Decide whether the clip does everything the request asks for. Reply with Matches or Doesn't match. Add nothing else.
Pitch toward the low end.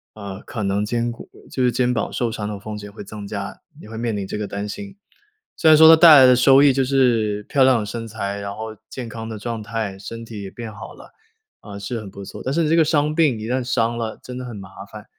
Matches